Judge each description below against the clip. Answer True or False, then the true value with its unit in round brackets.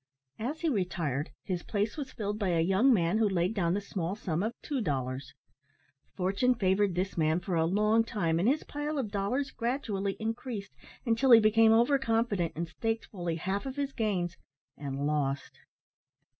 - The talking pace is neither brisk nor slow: True (180 wpm)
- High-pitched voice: True (200 Hz)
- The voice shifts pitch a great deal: False (4.9 semitones)